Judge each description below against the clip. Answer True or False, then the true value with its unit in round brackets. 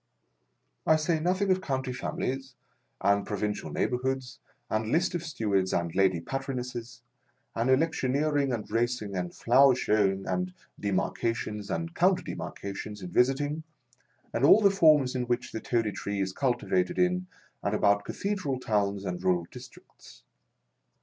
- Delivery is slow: False (145 wpm)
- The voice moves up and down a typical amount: False (6.2 semitones)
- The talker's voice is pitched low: True (125 Hz)